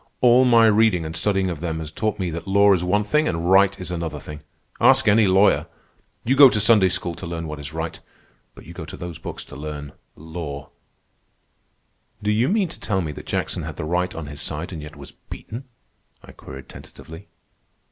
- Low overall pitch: Yes, very low, 90 Hz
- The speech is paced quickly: Yes, fast, 210 wpm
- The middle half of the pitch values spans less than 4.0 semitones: No, average, 4.7 semitones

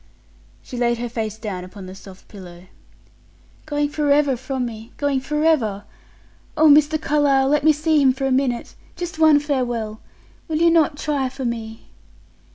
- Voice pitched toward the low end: No, very high, 270 Hz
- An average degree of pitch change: Yes, average, 4.8 semitones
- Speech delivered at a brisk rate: No, average, 165 wpm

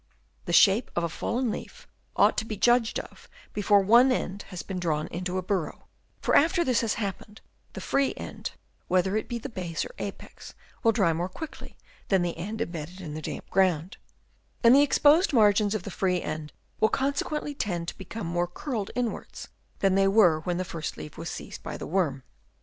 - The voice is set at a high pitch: Yes, high, 195 Hz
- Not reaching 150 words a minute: No, average, 200 wpm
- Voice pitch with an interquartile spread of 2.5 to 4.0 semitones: No, average, 4.9 semitones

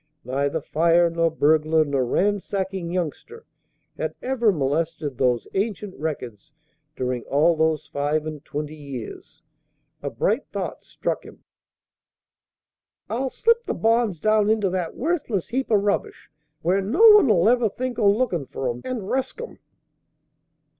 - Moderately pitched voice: Yes, medium, 175 Hz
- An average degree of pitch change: No, wide, 6.8 semitones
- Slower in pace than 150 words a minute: Yes, average, 140 wpm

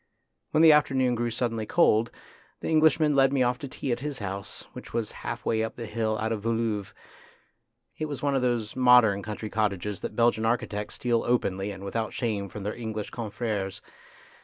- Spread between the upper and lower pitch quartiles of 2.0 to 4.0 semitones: Yes, average, 2.9 semitones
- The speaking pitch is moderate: No, low, 115 Hz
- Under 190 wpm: No, average, 195 wpm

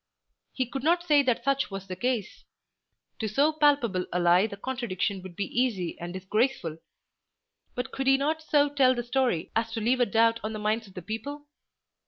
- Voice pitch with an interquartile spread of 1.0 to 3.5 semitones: No, wide, 5.4 semitones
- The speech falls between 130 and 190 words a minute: No, average, 200 wpm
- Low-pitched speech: No, high, 235 Hz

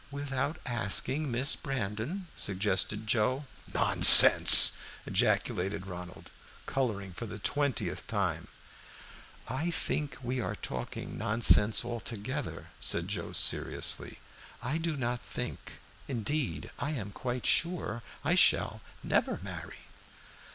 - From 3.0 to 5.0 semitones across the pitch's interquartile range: No, wide, 5.6 semitones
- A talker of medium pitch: No, low, 120 Hz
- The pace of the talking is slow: Yes, slow, 110 wpm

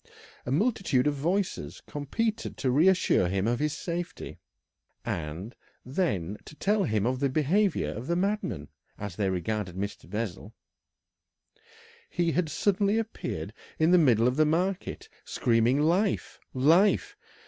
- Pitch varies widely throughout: Yes, wide, 8.9 semitones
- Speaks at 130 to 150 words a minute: Yes, slow, 135 wpm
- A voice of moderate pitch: Yes, medium, 145 Hz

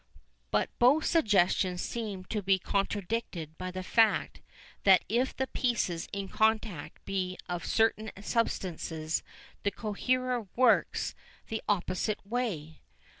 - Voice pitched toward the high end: Yes, high, 205 Hz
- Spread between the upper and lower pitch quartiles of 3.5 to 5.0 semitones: Yes, average, 4.0 semitones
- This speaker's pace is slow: Yes, slow, 120 wpm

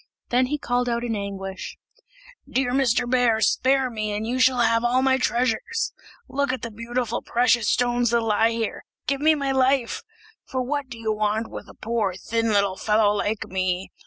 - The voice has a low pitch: No, high, 235 Hz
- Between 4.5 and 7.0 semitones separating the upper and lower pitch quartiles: No, average, 2.8 semitones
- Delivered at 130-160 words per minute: No, average, 190 wpm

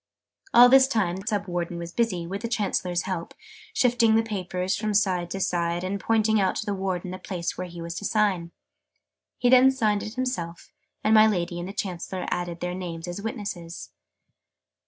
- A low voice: No, high, 190 Hz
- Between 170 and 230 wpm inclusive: Yes, average, 195 wpm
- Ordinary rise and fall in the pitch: Yes, average, 3.7 semitones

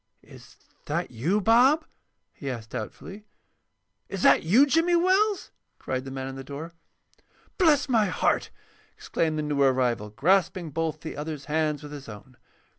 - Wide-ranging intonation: Yes, wide, 8.1 semitones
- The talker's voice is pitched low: No, medium, 155 Hz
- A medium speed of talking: Yes, average, 155 wpm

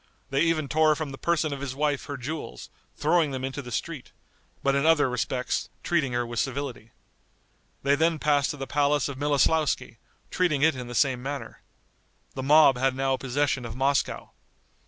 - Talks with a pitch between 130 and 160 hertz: Yes, medium, 140 Hz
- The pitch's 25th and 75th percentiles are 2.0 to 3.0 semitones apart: Yes, narrow, 2.4 semitones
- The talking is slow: No, average, 180 wpm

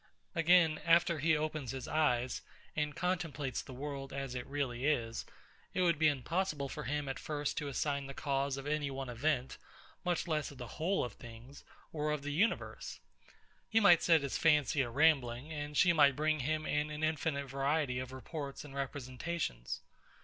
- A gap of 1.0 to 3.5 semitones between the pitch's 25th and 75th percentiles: Yes, average, 2.7 semitones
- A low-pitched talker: No, medium, 145 Hz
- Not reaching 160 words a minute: No, average, 180 wpm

